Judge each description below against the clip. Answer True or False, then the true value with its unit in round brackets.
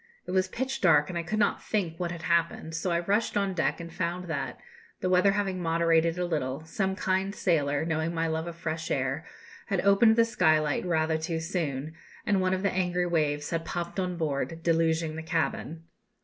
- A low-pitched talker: False (170 Hz)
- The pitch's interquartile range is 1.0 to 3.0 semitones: True (2.5 semitones)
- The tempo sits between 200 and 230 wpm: True (205 wpm)